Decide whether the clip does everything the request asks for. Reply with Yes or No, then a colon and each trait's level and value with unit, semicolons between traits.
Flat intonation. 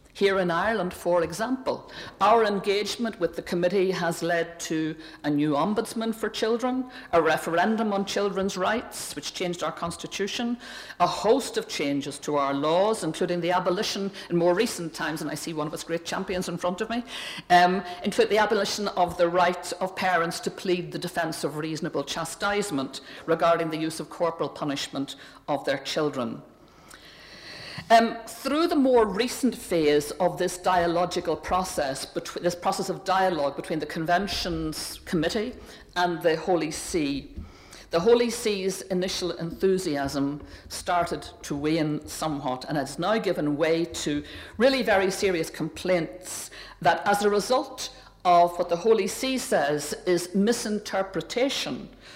No: average, 4.0 semitones